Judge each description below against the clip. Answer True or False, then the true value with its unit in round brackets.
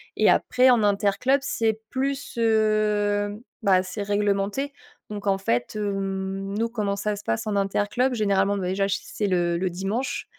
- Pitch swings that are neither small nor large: False (2.0 semitones)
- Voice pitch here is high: True (205 Hz)